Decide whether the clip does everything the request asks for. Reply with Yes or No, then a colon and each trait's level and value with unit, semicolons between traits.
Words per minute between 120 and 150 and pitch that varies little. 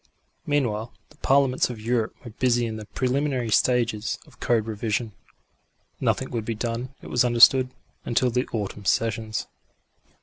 Yes: average, 145 wpm; narrow, 2.3 semitones